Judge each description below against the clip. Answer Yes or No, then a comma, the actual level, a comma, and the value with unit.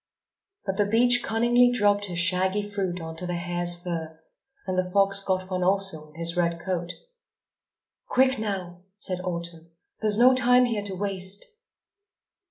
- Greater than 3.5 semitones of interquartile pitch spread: No, average, 2.9 semitones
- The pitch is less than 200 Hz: Yes, high, 190 Hz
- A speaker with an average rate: Yes, average, 160 wpm